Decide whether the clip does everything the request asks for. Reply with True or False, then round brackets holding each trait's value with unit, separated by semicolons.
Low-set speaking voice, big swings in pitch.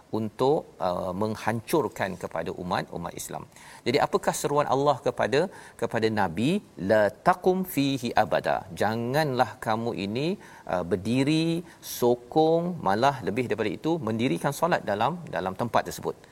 True (130 Hz; 6.4 semitones)